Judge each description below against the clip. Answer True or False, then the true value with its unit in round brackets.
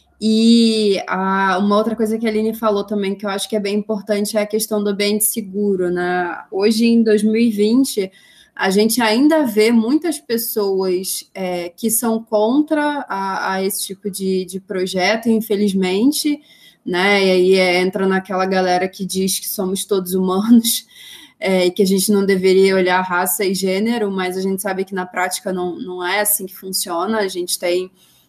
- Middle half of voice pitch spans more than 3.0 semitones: False (2.6 semitones)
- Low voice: False (200 Hz)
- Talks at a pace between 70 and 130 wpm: False (180 wpm)